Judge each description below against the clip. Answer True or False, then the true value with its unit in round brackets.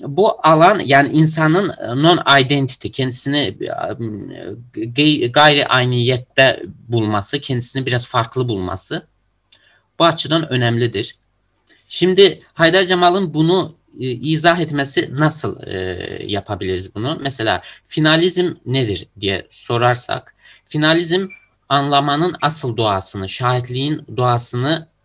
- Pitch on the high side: False (135 Hz)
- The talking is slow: True (90 wpm)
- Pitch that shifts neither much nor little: True (4.8 semitones)